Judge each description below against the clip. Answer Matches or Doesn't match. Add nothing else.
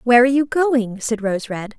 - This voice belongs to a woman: Matches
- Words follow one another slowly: Doesn't match